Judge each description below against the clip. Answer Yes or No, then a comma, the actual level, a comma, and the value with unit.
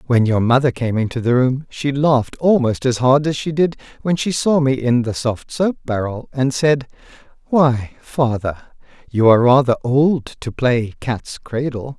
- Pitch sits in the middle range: No, low, 130 Hz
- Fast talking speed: No, average, 180 wpm